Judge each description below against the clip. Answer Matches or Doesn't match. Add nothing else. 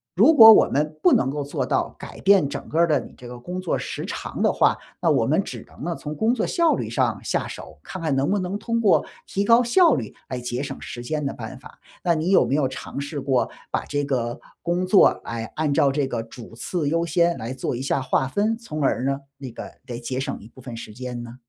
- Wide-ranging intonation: Matches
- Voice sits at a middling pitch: Matches